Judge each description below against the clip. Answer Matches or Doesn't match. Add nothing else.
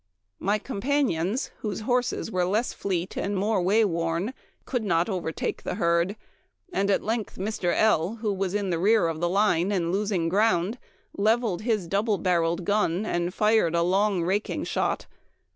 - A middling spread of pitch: Matches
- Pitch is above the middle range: Matches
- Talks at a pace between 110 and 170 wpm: Matches